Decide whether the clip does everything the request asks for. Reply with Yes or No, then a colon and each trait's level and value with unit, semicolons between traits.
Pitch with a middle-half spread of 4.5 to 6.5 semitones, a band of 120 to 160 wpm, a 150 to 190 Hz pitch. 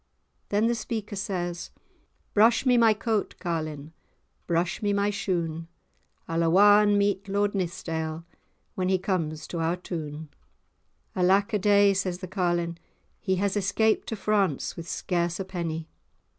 No: average, 3.3 semitones; average, 145 wpm; medium, 185 Hz